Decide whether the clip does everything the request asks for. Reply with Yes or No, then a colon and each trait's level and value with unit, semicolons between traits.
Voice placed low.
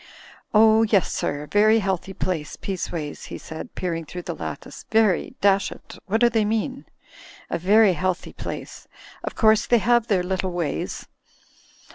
No: high, 195 Hz